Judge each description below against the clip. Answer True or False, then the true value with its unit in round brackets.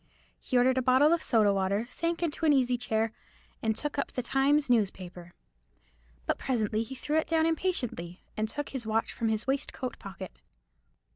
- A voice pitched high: True (245 Hz)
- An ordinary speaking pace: True (180 wpm)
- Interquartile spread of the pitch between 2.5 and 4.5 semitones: False (5.0 semitones)